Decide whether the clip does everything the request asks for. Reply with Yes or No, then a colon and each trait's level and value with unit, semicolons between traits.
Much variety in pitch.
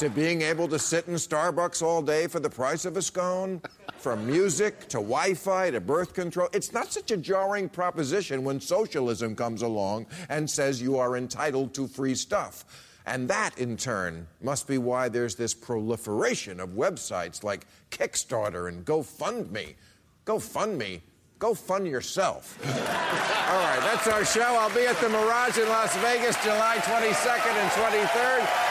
Yes: wide, 8.2 semitones